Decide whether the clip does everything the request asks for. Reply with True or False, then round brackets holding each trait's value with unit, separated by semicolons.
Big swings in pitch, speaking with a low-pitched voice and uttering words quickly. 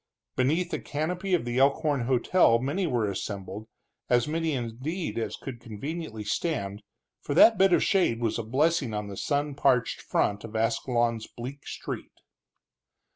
False (5.8 semitones; 125 Hz; 155 wpm)